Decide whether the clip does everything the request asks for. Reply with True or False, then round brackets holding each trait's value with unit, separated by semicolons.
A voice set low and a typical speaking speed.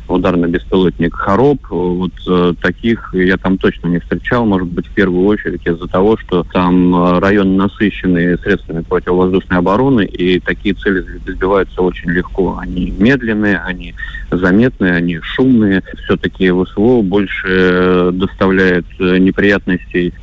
True (90 Hz; 135 wpm)